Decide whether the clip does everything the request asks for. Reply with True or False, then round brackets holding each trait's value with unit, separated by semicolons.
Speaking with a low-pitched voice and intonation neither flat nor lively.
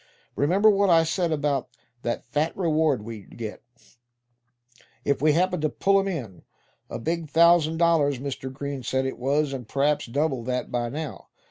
False (145 Hz; 3.9 semitones)